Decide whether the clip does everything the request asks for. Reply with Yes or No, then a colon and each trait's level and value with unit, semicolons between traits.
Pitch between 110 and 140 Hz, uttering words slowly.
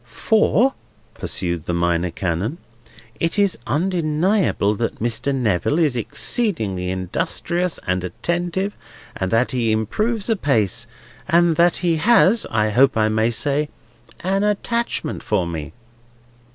Yes: low, 135 Hz; slow, 115 wpm